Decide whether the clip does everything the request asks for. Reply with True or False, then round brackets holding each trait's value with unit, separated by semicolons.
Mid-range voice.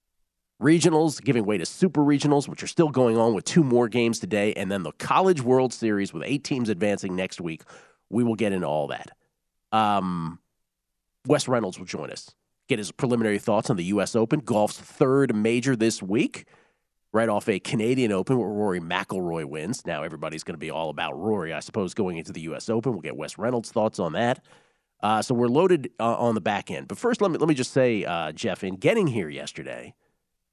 False (115 Hz)